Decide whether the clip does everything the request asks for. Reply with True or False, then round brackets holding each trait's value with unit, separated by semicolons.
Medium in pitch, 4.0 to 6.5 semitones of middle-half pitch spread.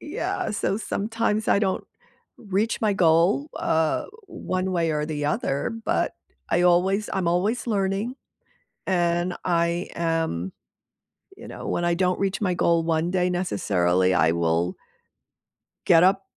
False (175 Hz; 3.3 semitones)